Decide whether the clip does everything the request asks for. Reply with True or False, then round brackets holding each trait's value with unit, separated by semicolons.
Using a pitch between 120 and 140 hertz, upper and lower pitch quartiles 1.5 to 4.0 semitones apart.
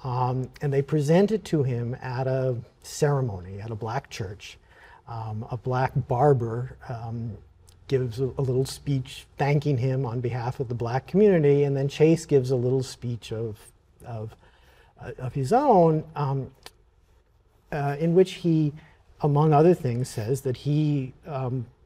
True (130 Hz; 3.3 semitones)